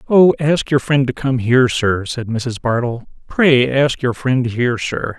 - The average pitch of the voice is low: Yes, low, 130 Hz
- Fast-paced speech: No, average, 195 wpm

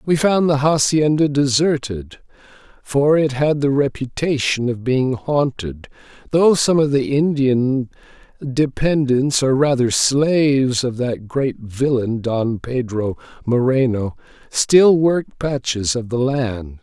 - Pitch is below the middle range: Yes, low, 130 Hz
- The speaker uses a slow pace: Yes, slow, 125 wpm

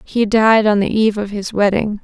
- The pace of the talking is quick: Yes, fast, 235 wpm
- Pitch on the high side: Yes, high, 210 Hz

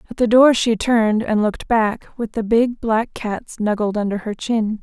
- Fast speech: Yes, fast, 210 wpm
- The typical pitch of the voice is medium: No, high, 220 Hz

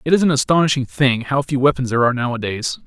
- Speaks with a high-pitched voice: No, low, 135 Hz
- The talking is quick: Yes, fast, 230 wpm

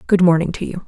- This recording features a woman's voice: Yes, female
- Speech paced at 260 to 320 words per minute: Yes, fast, 275 wpm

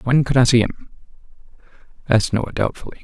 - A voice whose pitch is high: No, low, 120 Hz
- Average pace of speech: Yes, average, 160 wpm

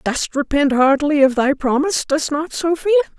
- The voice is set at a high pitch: Yes, very high, 285 Hz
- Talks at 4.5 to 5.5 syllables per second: Yes, 5.3 syllables/s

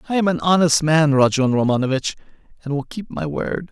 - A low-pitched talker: No, medium, 150 Hz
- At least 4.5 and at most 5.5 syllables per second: No, 5.7 syllables/s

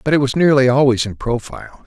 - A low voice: Yes, low, 130 Hz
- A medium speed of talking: No, fast, 225 wpm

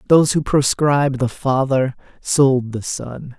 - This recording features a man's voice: Yes, male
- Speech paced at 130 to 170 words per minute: Yes, average, 140 wpm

